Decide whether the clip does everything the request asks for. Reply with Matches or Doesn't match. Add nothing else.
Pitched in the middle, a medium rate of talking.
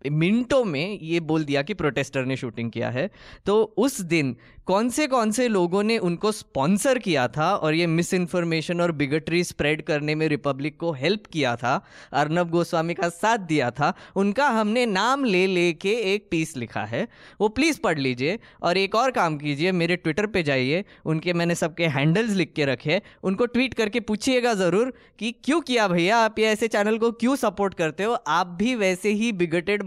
Doesn't match